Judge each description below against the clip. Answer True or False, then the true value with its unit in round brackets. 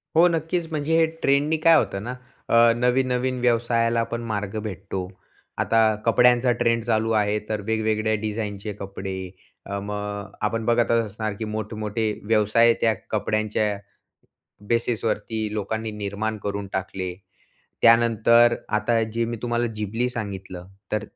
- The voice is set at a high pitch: False (110 Hz)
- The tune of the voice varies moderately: False (2.2 semitones)